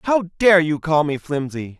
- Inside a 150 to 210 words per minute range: Yes, average, 200 wpm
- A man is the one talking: Yes, male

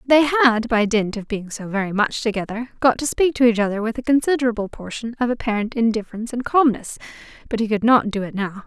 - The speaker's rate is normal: No, fast, 220 wpm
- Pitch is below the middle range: No, high, 230 Hz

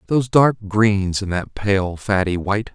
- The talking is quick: No, average, 175 wpm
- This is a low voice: Yes, low, 100 Hz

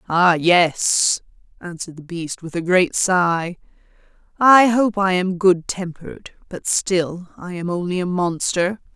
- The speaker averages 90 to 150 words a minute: Yes, average, 145 wpm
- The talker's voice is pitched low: No, medium, 180 Hz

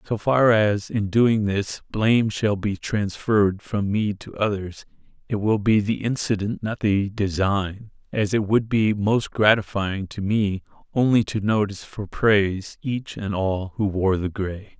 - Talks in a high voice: No, low, 105 Hz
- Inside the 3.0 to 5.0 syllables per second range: Yes, 4.1 syllables/s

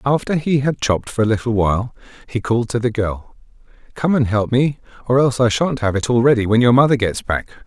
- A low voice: Yes, low, 120 Hz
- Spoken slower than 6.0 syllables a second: No, 6.1 syllables/s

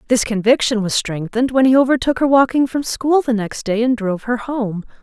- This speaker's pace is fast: Yes, fast, 215 wpm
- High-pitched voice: Yes, high, 240 Hz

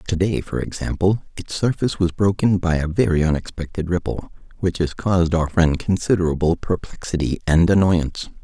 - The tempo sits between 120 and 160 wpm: Yes, average, 150 wpm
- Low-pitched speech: Yes, very low, 85 Hz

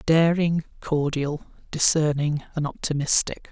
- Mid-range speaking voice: Yes, medium, 155 Hz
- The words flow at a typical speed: No, slow, 85 wpm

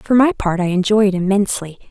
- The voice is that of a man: No, female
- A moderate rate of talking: No, fast, 220 wpm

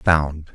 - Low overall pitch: Yes, very low, 80 Hz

